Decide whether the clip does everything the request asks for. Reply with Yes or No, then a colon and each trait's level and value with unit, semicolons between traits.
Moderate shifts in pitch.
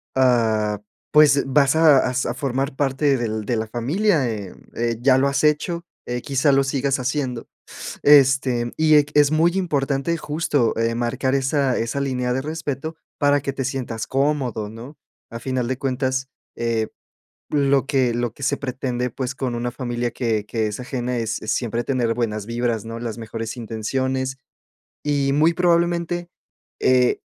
Yes: average, 3.1 semitones